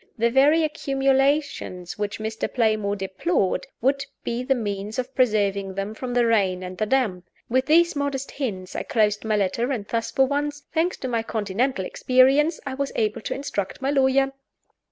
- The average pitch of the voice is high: Yes, high, 245 Hz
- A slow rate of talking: No, average, 175 wpm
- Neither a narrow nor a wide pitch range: Yes, average, 4.9 semitones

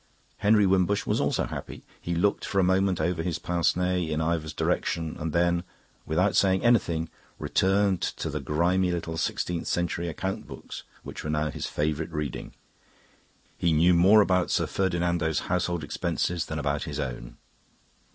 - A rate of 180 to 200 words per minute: No, average, 160 wpm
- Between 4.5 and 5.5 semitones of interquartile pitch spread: No, average, 2.7 semitones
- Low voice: Yes, very low, 85 Hz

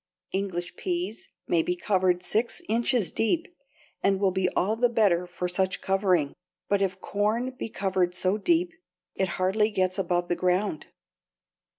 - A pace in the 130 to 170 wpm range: Yes, average, 155 wpm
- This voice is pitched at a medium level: No, high, 195 Hz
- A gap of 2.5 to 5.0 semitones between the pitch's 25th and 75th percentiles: Yes, average, 3.3 semitones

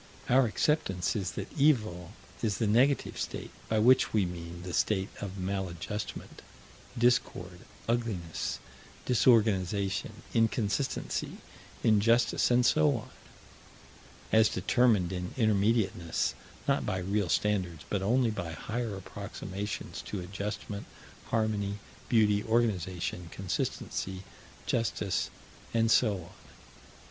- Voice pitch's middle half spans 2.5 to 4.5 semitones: Yes, average, 3.5 semitones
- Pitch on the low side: Yes, low, 105 Hz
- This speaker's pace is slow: Yes, slow, 105 wpm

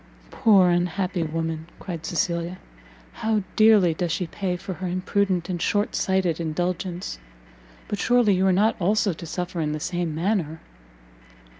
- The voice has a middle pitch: Yes, medium, 180 Hz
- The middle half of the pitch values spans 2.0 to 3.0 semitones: Yes, average, 2.7 semitones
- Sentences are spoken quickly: No, average, 150 wpm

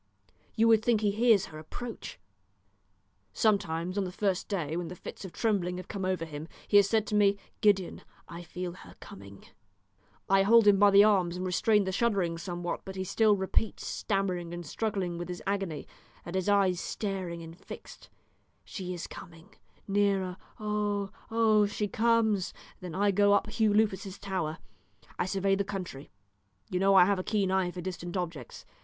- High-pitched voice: Yes, high, 195 Hz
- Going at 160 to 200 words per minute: Yes, average, 180 wpm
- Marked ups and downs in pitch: No, average, 2.7 semitones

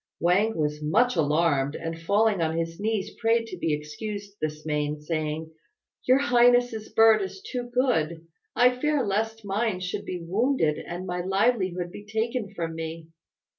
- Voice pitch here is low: No, high, 190 Hz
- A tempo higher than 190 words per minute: No, average, 160 wpm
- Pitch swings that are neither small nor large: No, wide, 5.7 semitones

